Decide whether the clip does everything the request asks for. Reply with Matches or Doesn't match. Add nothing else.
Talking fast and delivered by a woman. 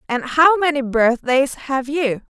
Doesn't match